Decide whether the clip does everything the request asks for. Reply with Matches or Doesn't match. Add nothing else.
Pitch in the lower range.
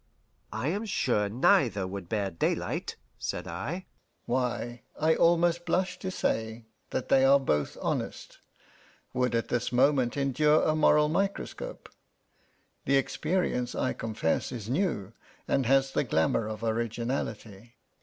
Matches